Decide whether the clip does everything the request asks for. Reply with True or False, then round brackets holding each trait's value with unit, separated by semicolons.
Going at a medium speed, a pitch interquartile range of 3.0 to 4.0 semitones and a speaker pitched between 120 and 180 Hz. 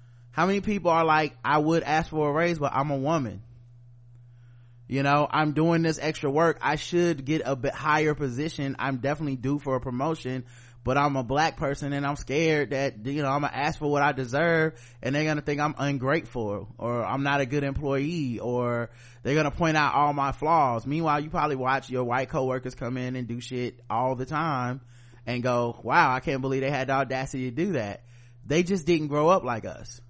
False (220 wpm; 3.4 semitones; 140 Hz)